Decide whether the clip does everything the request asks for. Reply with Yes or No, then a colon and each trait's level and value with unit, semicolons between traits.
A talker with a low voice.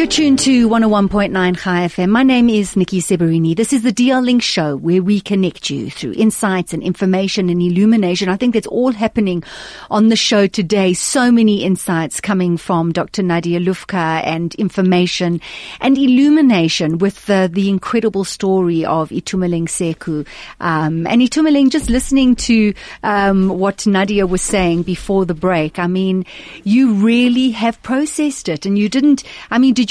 No: high, 195 Hz